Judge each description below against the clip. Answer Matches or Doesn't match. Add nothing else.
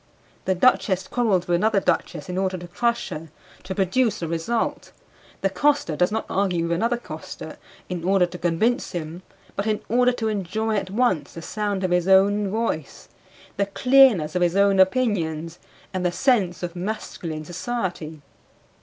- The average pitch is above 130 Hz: Matches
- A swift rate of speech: Doesn't match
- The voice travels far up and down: Doesn't match